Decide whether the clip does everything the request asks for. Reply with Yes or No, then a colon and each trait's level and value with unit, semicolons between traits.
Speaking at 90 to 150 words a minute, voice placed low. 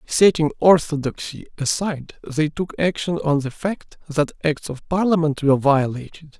No: average, 140 wpm; medium, 155 Hz